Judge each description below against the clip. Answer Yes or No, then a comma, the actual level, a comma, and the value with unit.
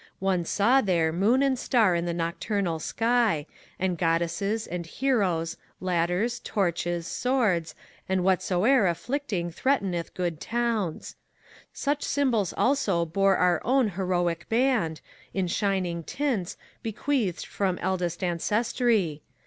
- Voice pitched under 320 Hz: Yes, high, 190 Hz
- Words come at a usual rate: No, slow, 115 wpm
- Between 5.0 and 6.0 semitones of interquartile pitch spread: Yes, average, 5.3 semitones